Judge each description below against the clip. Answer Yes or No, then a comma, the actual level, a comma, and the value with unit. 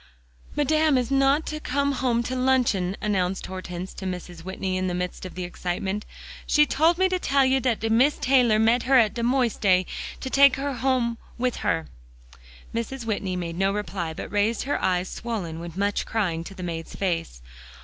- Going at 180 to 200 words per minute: Yes, average, 190 wpm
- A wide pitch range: Yes, wide, 6.1 semitones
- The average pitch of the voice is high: Yes, high, 220 Hz